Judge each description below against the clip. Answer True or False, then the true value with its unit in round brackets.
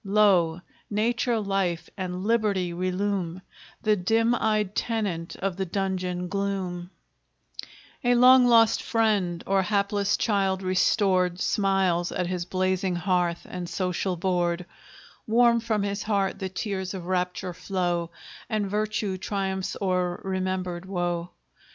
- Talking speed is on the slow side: True (125 wpm)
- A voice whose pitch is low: False (190 Hz)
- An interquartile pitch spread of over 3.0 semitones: False (2.4 semitones)